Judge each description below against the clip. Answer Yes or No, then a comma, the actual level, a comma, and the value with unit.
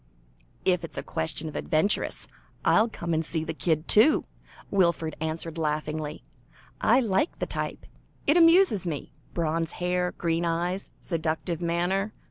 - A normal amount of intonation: Yes, average, 3.1 semitones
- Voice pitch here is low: No, medium, 170 Hz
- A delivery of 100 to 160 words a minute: Yes, average, 140 wpm